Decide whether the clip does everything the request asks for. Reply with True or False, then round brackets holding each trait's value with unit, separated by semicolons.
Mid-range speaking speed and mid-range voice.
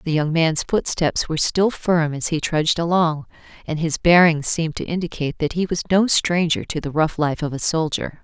False (210 wpm; 160 Hz)